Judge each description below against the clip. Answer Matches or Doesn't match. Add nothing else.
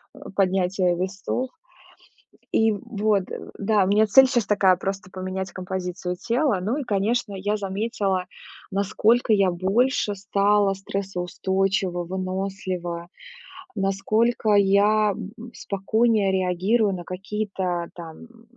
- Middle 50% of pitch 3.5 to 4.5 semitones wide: Doesn't match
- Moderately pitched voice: Doesn't match